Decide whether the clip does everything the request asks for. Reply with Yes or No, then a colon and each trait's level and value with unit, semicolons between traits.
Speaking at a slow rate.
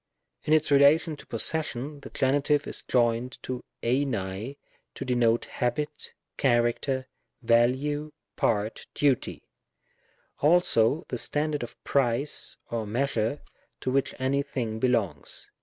Yes: slow, 115 wpm